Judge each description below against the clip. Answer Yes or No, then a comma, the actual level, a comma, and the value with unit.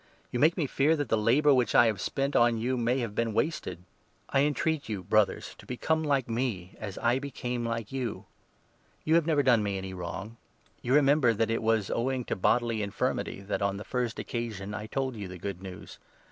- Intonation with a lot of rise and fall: No, average, 4.4 semitones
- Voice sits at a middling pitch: No, low, 115 Hz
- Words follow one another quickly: Yes, fast, 240 wpm